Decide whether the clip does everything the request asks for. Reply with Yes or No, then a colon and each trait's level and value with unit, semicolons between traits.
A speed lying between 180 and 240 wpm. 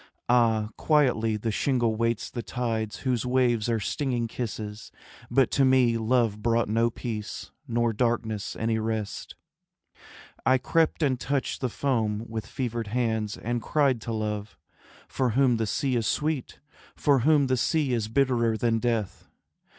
No: average, 150 wpm